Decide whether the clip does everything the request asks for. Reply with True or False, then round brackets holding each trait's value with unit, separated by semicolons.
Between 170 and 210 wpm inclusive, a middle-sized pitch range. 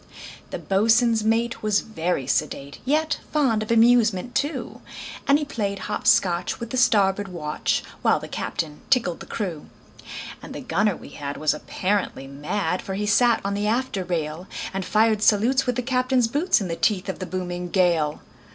True (180 wpm; 4.8 semitones)